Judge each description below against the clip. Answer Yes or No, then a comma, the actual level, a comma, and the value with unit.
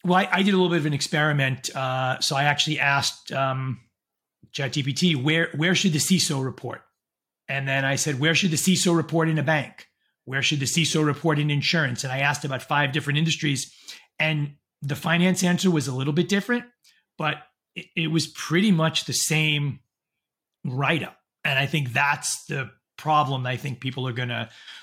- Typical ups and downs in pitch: Yes, average, 3.2 semitones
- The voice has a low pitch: No, medium, 150 Hz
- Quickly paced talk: No, average, 190 wpm